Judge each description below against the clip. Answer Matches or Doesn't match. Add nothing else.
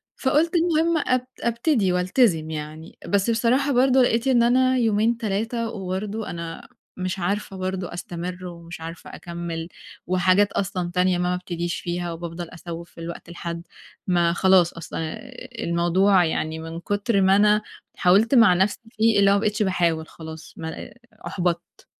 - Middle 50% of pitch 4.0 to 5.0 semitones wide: Matches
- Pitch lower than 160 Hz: Doesn't match